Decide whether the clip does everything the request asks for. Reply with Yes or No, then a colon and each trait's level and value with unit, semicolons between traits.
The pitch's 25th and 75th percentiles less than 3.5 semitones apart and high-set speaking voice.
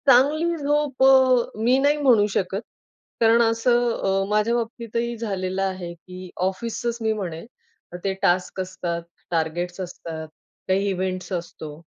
No: average, 4.6 semitones; high, 205 Hz